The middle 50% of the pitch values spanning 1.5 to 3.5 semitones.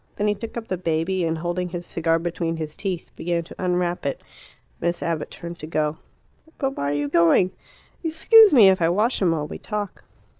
Yes: average, 2.8 semitones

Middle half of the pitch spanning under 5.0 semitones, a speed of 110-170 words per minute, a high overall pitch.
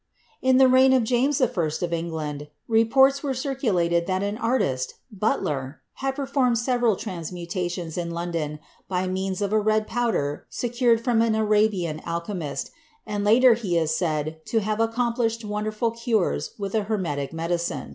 No: wide, 5.6 semitones; average, 160 wpm; high, 210 Hz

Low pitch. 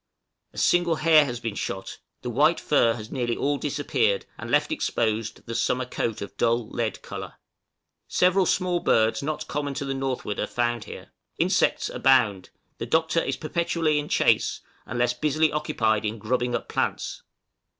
Yes: low, 130 Hz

